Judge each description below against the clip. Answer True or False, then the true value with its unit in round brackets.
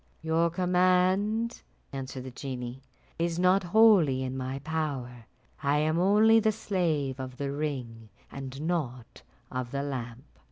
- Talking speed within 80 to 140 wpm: True (135 wpm)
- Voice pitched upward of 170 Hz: False (145 Hz)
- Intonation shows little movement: False (5.6 semitones)